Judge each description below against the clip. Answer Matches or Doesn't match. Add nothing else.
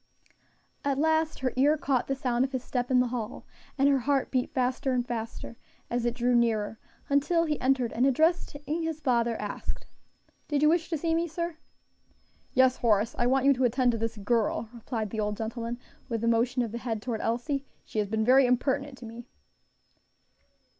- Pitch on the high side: Matches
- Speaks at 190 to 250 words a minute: Matches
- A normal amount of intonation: Matches